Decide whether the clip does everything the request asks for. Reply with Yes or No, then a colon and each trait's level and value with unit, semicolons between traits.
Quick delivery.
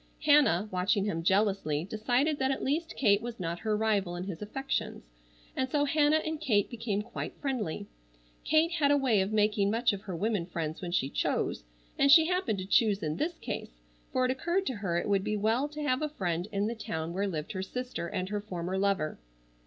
Yes: fast, 215 wpm